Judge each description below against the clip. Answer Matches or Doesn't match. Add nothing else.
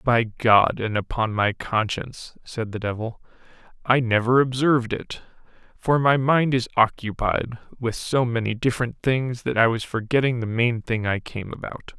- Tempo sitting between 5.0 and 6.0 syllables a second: Doesn't match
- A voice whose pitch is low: Matches